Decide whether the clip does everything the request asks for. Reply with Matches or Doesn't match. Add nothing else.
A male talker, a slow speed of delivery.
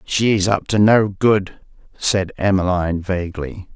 Matches